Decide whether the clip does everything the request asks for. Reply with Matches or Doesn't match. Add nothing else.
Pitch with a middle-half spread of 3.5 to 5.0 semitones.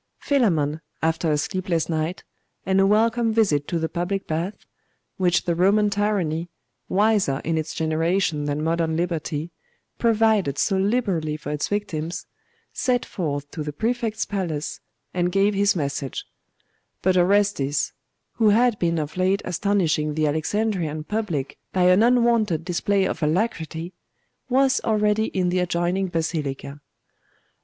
Matches